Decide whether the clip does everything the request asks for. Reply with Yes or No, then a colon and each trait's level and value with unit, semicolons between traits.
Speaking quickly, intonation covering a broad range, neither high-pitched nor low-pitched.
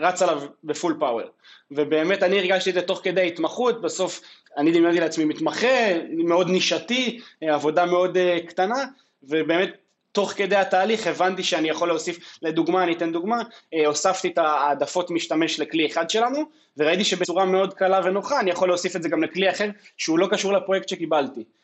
No: fast, 165 wpm; average, 2.7 semitones; medium, 180 Hz